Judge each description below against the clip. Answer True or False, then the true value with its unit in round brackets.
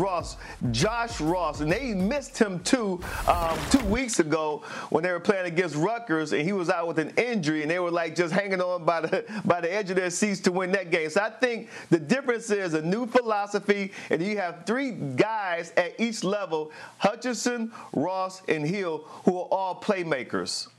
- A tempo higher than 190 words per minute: True (200 wpm)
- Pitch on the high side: True (195 Hz)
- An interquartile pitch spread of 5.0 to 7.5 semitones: False (4.3 semitones)